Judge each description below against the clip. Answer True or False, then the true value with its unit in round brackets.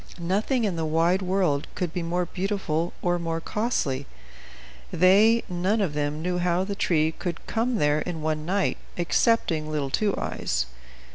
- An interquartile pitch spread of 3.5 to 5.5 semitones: True (3.8 semitones)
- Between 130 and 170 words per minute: True (160 wpm)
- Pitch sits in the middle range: True (175 Hz)